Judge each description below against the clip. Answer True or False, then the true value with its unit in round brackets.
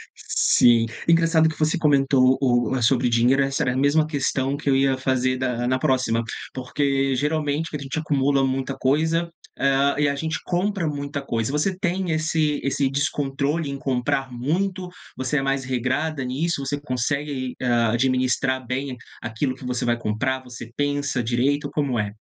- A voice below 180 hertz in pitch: True (135 Hz)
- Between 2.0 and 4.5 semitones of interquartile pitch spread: True (2.6 semitones)